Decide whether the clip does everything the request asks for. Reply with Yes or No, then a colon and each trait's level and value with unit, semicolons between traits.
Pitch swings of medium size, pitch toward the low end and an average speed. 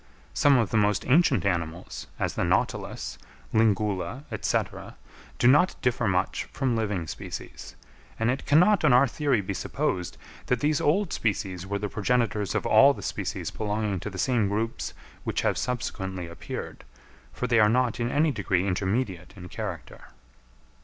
Yes: average, 4.7 semitones; low, 110 Hz; average, 160 wpm